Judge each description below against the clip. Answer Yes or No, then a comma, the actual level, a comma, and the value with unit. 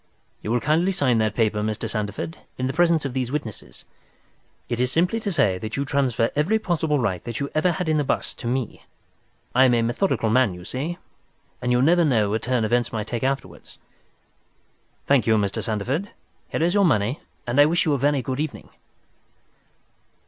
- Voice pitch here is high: No, low, 130 Hz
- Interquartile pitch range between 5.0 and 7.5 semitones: Yes, wide, 5.5 semitones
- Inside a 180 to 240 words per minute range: Yes, average, 200 wpm